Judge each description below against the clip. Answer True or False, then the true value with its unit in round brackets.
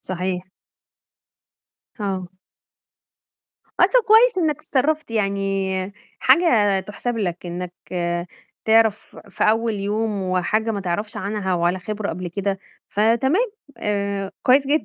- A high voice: True (210 Hz)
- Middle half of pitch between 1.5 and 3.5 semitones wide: False (3.9 semitones)